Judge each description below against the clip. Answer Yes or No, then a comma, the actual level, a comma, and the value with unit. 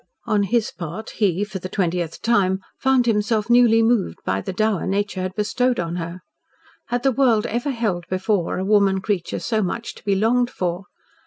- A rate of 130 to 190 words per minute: Yes, average, 185 wpm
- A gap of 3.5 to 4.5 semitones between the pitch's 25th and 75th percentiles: Yes, average, 4.0 semitones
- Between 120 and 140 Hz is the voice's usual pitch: No, high, 205 Hz